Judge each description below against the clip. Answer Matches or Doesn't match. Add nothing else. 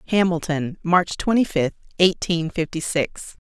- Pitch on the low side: Doesn't match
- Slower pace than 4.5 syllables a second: Matches